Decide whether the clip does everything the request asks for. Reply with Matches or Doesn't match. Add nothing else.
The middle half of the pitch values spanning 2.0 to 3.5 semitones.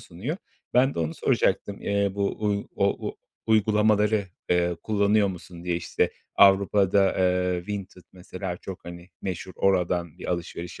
Matches